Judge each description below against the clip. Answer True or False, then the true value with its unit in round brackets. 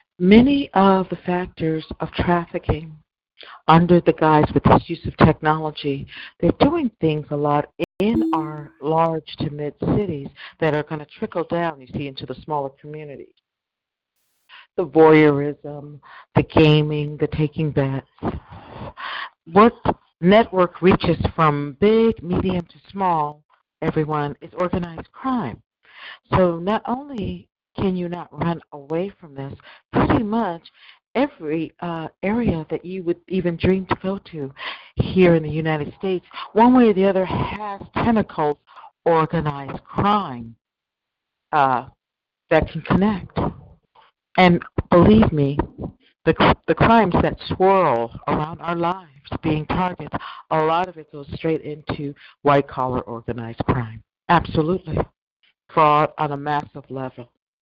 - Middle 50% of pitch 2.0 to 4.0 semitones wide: True (3.7 semitones)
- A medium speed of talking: False (130 wpm)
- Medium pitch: True (160 Hz)